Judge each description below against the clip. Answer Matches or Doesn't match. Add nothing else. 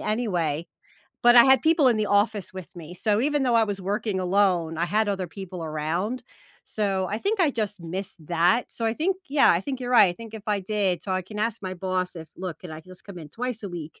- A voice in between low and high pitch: Doesn't match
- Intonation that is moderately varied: Matches